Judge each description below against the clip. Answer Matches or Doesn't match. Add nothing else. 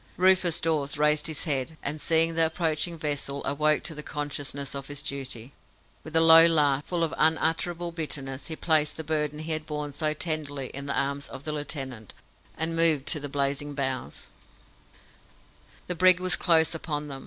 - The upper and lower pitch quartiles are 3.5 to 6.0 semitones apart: Doesn't match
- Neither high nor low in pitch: Matches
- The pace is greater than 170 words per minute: Matches